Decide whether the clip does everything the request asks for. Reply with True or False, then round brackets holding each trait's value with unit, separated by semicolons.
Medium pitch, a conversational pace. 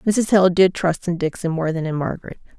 False (175 Hz; 230 wpm)